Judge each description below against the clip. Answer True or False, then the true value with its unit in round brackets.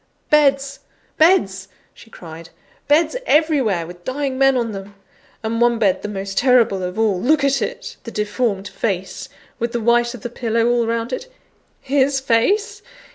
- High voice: True (235 Hz)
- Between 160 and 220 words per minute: True (165 wpm)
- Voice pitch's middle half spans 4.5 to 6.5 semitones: True (5.0 semitones)